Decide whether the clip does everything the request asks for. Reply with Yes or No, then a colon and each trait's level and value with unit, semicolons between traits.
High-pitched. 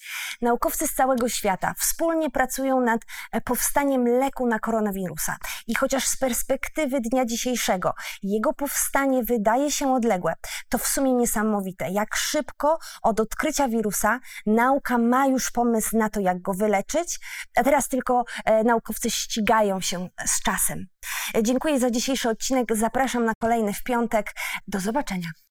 Yes: high, 240 Hz